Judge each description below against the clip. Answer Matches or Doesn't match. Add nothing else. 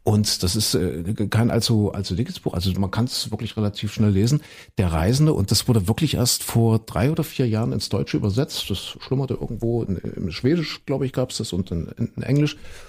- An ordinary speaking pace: Doesn't match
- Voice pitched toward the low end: Matches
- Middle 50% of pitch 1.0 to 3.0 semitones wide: Doesn't match